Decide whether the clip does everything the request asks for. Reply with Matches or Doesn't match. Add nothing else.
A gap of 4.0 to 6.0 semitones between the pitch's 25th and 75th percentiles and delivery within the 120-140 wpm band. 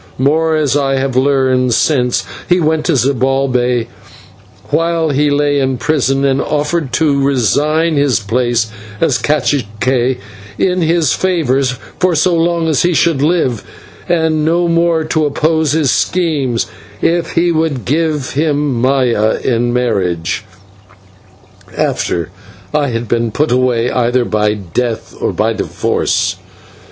Matches